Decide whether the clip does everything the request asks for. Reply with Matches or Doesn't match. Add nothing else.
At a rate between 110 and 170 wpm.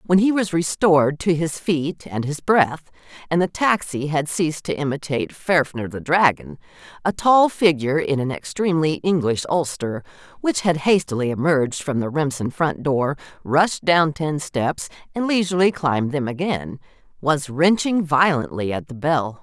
Matches